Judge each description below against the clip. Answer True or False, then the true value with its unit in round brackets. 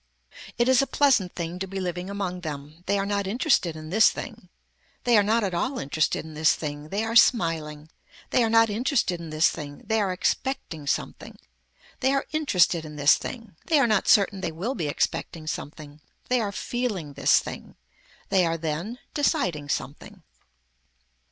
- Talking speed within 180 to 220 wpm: True (185 wpm)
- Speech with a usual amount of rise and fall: False (6.3 semitones)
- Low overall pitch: False (185 Hz)